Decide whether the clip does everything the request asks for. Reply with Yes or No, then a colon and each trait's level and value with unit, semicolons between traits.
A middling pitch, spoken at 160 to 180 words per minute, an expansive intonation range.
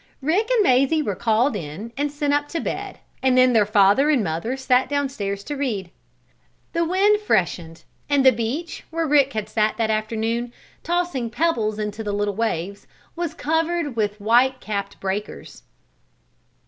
No: high, 240 Hz; average, 165 wpm; wide, 5.7 semitones